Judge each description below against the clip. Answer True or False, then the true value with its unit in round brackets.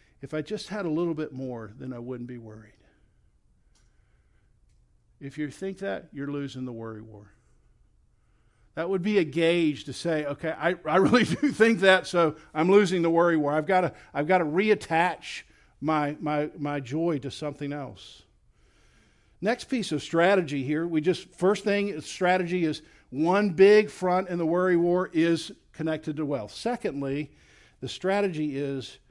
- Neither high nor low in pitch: True (155 Hz)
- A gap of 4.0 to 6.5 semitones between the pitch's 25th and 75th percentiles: True (4.9 semitones)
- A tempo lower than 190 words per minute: True (170 wpm)